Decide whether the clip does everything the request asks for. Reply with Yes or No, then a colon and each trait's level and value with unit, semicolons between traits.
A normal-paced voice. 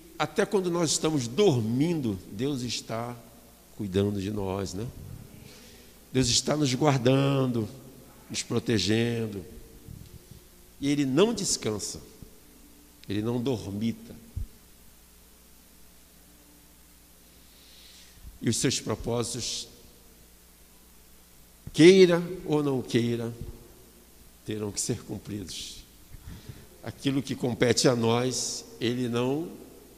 No: slow, 85 wpm